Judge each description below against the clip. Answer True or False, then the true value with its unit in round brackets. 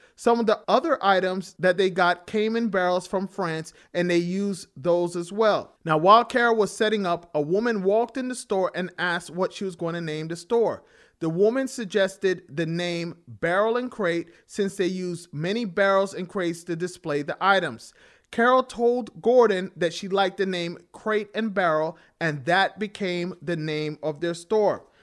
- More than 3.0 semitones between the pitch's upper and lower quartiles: True (3.8 semitones)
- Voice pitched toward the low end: False (185 Hz)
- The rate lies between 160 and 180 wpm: False (190 wpm)